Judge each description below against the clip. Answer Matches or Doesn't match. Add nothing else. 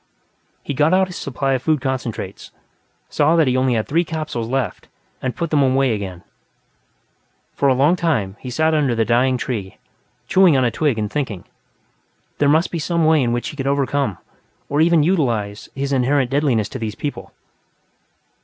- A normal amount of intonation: Matches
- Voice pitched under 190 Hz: Matches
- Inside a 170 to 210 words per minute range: Matches